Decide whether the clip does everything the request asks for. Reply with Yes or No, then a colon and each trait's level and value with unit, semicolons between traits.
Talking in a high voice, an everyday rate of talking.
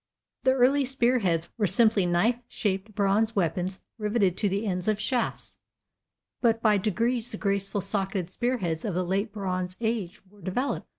Yes: high, 205 Hz; average, 170 wpm